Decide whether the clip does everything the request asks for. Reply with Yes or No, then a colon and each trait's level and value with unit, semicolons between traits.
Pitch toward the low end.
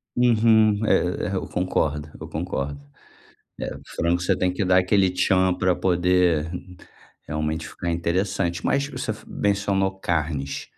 Yes: very low, 90 Hz